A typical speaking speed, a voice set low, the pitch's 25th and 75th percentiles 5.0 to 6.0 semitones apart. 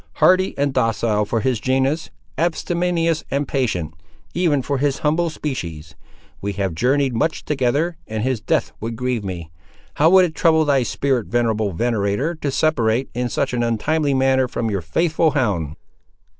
Yes: average, 160 wpm; low, 130 Hz; wide, 5.5 semitones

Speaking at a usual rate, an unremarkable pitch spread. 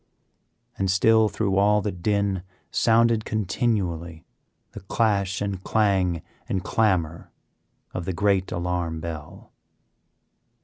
No: slow, 105 wpm; average, 3.2 semitones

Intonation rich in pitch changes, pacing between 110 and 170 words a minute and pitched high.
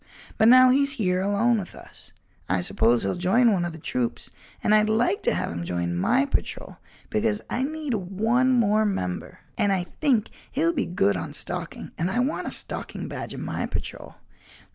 No: wide, 6.3 semitones; average, 190 wpm; high, 215 Hz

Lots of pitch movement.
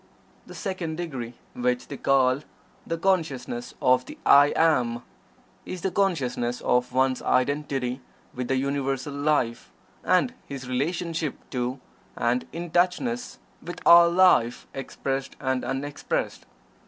No: average, 4.8 semitones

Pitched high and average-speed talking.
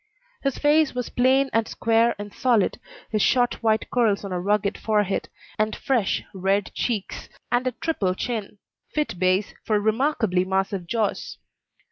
Yes: high, 220 Hz; average, 150 wpm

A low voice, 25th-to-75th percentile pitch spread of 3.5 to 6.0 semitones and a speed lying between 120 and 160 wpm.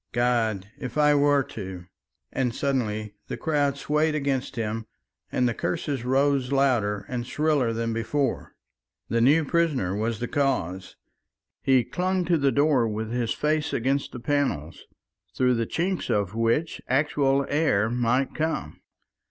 Yes: low, 130 Hz; average, 4.1 semitones; average, 145 wpm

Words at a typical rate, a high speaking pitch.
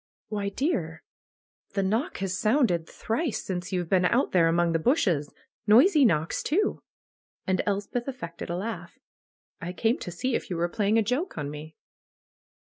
Yes: average, 165 wpm; high, 195 Hz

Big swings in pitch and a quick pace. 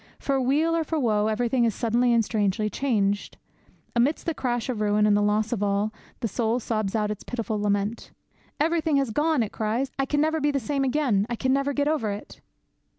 No: average, 4.7 semitones; fast, 215 wpm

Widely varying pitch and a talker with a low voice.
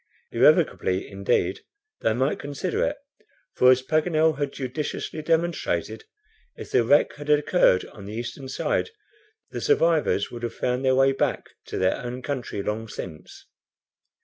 No: average, 4.7 semitones; low, 130 Hz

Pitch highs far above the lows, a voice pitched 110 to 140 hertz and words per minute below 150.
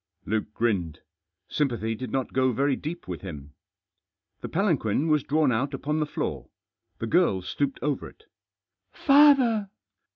Yes: wide, 6.1 semitones; low, 135 Hz; average, 140 wpm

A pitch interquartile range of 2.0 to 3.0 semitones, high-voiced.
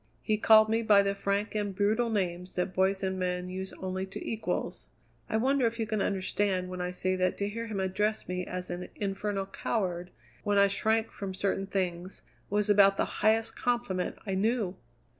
Yes: narrow, 2.5 semitones; high, 200 Hz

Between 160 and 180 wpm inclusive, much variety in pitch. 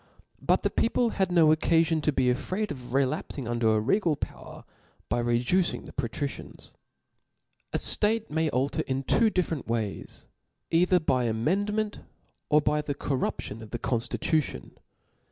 No: average, 150 wpm; wide, 6.8 semitones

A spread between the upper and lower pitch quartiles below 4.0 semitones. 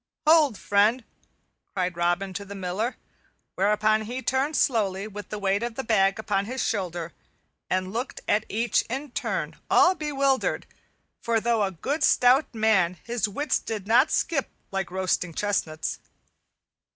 No: average, 4.3 semitones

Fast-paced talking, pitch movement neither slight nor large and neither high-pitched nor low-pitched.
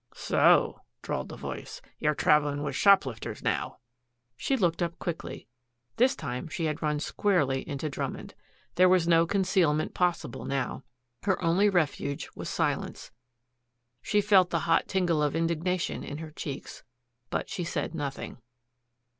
No: average, 145 wpm; average, 3.6 semitones; medium, 165 Hz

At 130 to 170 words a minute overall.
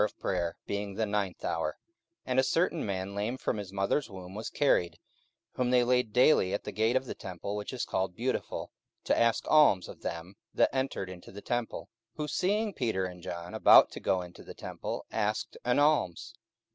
No: average, 185 wpm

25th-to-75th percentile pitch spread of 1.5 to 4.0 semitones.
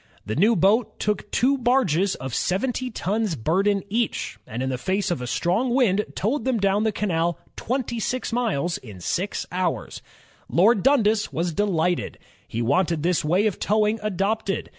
No: average, 4.5 semitones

